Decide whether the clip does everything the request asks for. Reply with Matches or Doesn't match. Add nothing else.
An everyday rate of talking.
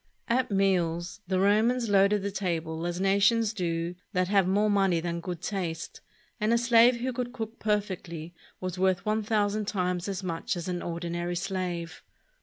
Matches